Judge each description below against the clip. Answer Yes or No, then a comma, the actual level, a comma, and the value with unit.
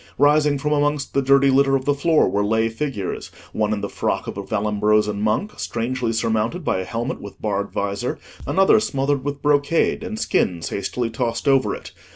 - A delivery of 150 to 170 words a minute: No, average, 190 wpm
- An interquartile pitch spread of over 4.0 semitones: Yes, average, 5.1 semitones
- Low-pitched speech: Yes, low, 130 Hz